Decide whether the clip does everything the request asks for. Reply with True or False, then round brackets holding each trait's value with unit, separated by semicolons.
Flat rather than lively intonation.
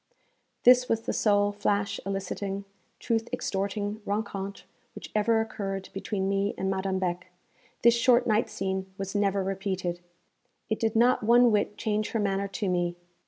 True (2.2 semitones)